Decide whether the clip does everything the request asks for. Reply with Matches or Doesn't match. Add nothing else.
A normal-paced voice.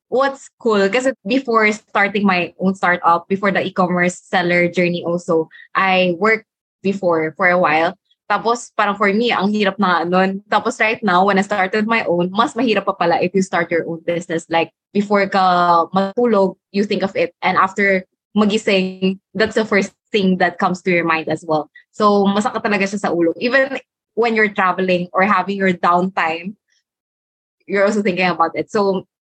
Doesn't match